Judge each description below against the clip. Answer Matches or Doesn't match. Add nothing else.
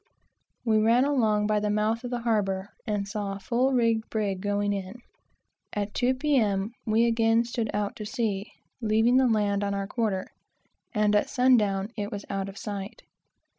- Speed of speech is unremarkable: Matches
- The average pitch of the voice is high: Matches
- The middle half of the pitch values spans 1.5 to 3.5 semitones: Matches